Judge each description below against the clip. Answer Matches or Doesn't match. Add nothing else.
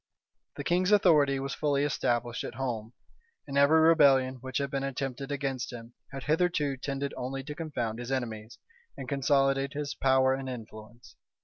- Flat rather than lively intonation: Matches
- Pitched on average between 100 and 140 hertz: Matches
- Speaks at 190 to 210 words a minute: Doesn't match